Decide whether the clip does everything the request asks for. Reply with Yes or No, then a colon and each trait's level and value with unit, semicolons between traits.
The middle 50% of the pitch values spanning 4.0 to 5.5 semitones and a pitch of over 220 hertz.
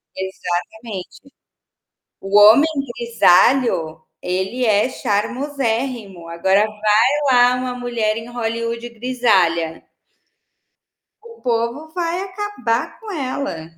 Yes: average, 4.4 semitones; high, 230 Hz